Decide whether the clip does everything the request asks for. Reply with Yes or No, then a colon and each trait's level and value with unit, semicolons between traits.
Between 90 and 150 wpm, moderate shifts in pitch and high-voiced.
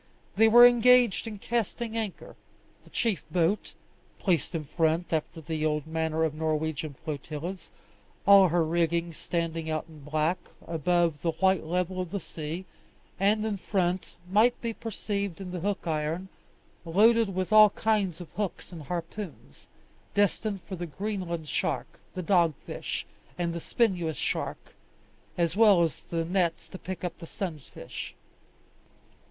No: average, 145 wpm; average, 3.8 semitones; medium, 175 Hz